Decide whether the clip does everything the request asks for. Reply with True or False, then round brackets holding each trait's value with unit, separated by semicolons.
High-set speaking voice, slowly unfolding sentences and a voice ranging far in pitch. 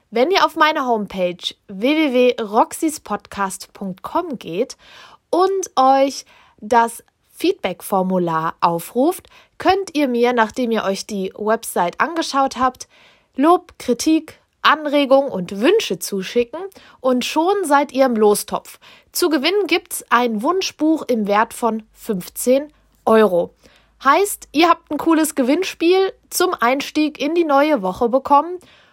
True (265 Hz; 120 wpm; 6.3 semitones)